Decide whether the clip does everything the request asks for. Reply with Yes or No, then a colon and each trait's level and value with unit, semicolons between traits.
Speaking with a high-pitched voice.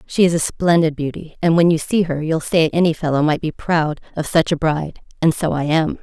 No: medium, 160 Hz